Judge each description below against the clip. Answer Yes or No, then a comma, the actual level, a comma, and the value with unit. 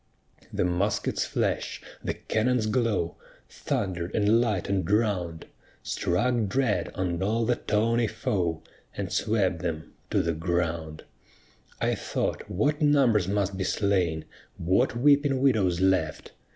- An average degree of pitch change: Yes, average, 4.7 semitones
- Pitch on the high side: No, low, 100 Hz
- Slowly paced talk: Yes, slow, 125 wpm